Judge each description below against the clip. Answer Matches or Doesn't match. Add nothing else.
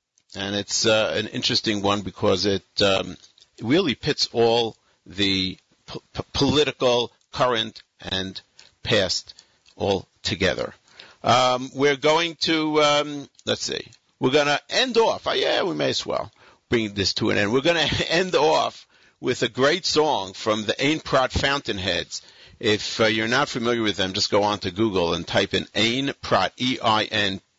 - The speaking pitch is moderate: Doesn't match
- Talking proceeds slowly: Doesn't match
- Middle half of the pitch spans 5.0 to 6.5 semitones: Matches